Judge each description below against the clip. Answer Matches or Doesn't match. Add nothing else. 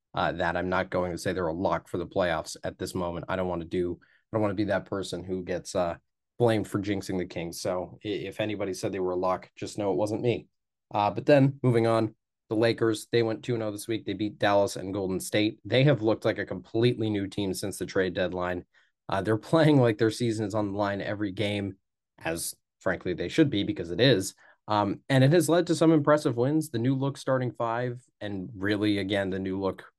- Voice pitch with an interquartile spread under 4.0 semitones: Matches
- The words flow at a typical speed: Doesn't match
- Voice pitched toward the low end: Matches